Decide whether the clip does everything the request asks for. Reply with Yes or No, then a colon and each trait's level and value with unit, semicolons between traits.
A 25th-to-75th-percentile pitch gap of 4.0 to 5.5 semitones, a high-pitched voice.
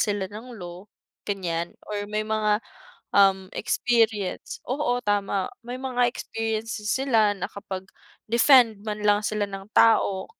No: narrow, 2.5 semitones; high, 210 Hz